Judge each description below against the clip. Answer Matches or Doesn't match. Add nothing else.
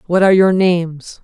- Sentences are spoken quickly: Doesn't match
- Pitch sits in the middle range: Matches